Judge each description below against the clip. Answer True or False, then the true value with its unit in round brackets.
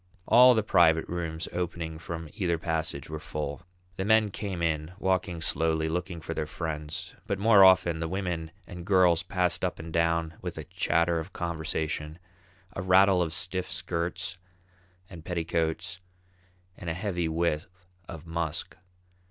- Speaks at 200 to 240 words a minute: False (150 wpm)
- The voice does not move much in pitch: True (2.2 semitones)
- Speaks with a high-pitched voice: False (85 Hz)